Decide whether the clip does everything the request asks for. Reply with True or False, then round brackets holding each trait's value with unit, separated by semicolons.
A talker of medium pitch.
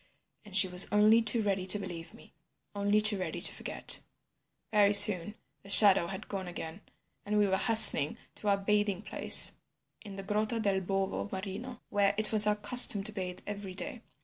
False (205 Hz)